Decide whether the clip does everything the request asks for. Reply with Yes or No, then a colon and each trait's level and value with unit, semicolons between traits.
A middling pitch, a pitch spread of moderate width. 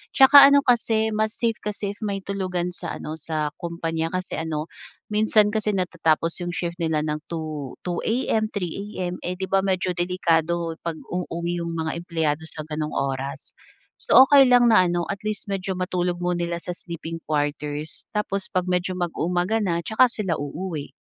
Yes: medium, 175 Hz; average, 3.4 semitones